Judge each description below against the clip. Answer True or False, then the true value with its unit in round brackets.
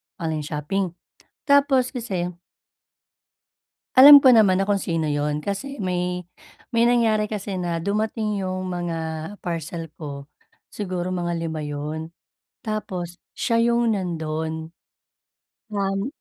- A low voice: False (185 Hz)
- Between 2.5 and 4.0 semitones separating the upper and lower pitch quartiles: False (4.5 semitones)